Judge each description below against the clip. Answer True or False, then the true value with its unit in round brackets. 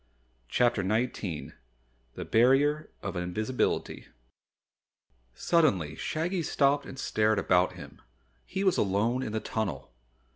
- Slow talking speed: True (110 wpm)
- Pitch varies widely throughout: True (6.6 semitones)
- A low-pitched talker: True (115 Hz)